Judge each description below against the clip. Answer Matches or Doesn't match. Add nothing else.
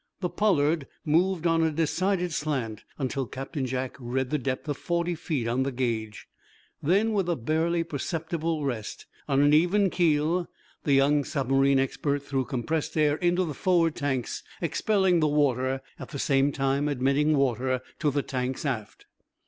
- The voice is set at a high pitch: Doesn't match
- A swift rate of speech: Doesn't match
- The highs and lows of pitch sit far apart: Doesn't match